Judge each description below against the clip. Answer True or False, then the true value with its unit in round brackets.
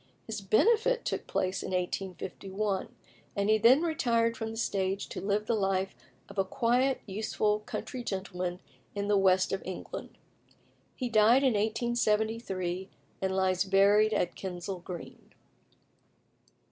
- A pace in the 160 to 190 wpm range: False (135 wpm)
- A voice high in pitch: True (205 Hz)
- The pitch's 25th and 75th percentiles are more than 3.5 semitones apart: False (3.2 semitones)